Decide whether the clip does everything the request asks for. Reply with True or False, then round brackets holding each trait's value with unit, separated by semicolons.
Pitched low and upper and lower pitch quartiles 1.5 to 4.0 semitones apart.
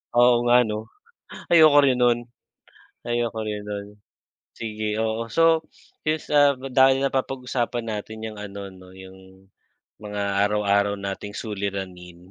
True (110 Hz; 3.5 semitones)